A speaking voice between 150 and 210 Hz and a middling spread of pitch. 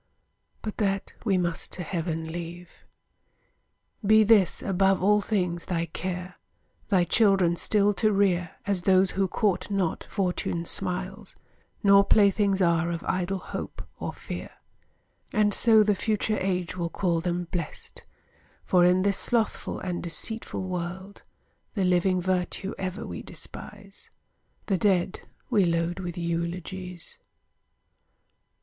No: medium, 185 Hz; narrow, 2.3 semitones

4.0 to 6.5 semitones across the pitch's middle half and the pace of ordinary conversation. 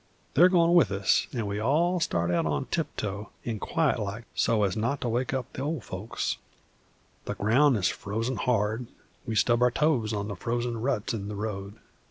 Yes: average, 4.5 semitones; average, 185 wpm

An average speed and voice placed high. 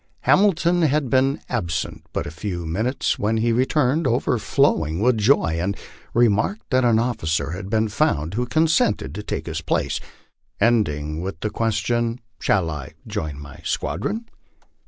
No: average, 155 wpm; low, 110 Hz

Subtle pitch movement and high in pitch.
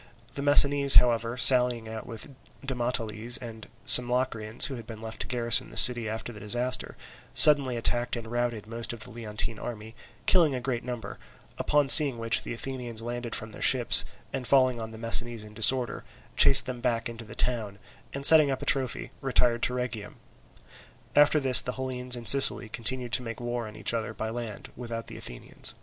No: narrow, 2.0 semitones; low, 120 Hz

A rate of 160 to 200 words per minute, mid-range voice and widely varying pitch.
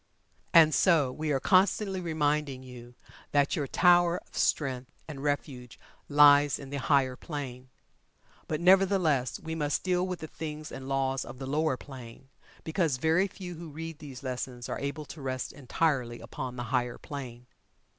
No: average, 165 wpm; medium, 145 Hz; average, 3.7 semitones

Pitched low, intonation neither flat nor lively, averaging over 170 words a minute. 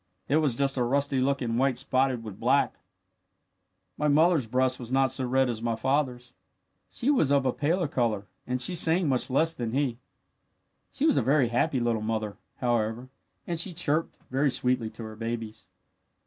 Yes: low, 130 Hz; average, 3.3 semitones; average, 180 wpm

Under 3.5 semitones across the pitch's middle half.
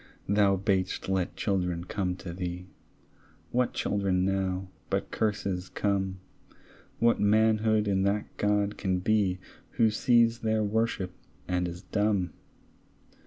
Yes: narrow, 2.6 semitones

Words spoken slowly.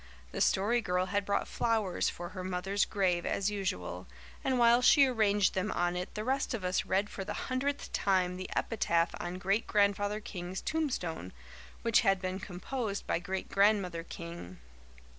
No: average, 170 wpm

